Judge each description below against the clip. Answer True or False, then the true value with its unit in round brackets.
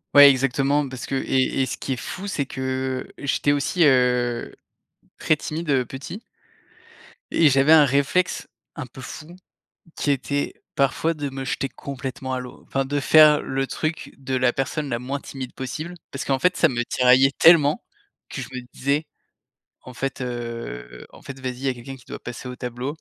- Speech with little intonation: True (2.2 semitones)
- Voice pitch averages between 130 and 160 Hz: True (135 Hz)